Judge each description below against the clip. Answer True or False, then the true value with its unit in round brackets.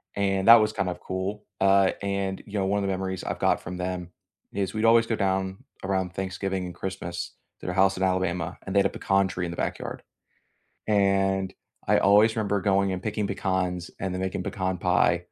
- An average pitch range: False (1.1 semitones)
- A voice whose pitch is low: True (95 Hz)